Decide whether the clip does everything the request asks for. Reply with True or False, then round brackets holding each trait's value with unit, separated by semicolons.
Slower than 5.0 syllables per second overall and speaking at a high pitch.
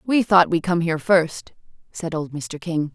False (4.5 syllables/s; 170 Hz)